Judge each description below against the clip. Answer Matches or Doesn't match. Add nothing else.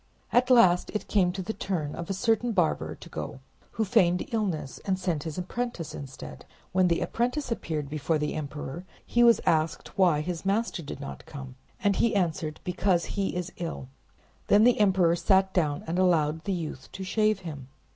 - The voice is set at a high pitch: Doesn't match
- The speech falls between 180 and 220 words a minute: Matches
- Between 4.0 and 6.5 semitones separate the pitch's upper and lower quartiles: Matches